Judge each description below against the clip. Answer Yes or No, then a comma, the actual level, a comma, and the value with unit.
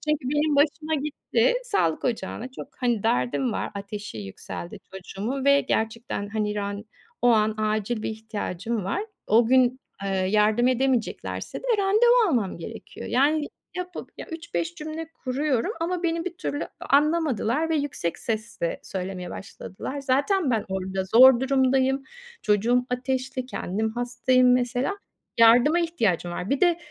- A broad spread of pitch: Yes, wide, 5.7 semitones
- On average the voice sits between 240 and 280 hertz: Yes, very high, 250 Hz